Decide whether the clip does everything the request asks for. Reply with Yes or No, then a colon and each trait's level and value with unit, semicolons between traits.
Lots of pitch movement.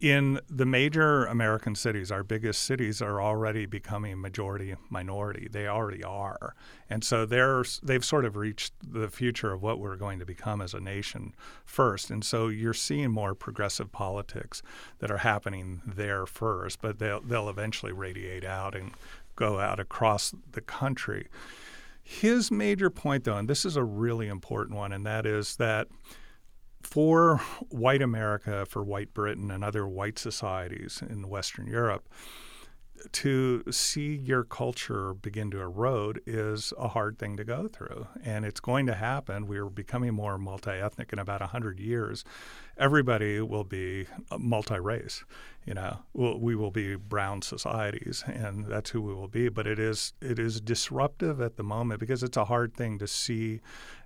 No: average, 3.0 semitones